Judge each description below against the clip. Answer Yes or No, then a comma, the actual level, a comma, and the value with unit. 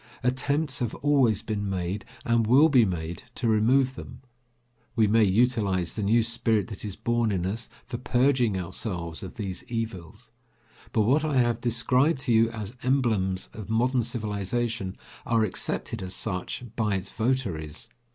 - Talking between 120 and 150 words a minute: No, average, 160 wpm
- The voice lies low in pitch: Yes, low, 115 Hz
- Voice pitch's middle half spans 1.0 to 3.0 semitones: No, average, 4.0 semitones